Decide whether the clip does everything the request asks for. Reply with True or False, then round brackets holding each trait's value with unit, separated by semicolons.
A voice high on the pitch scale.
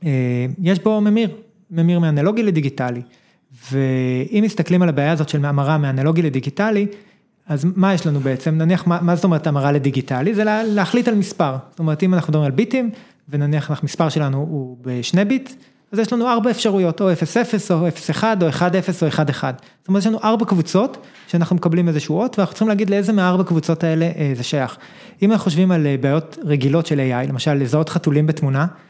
False (170 Hz)